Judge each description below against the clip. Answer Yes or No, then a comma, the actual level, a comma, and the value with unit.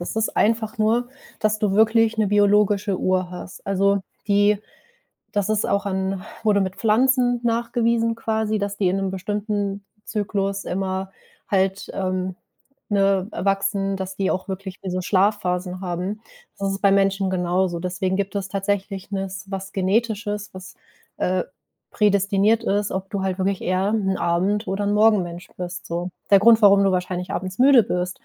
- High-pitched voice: Yes, high, 195 Hz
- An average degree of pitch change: No, narrow, 1.9 semitones